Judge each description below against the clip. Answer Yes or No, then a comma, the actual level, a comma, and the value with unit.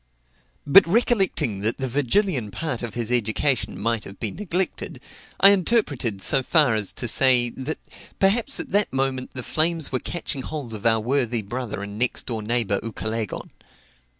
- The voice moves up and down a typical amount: No, wide, 6.1 semitones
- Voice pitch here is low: Yes, low, 125 Hz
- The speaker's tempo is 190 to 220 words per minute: No, average, 165 wpm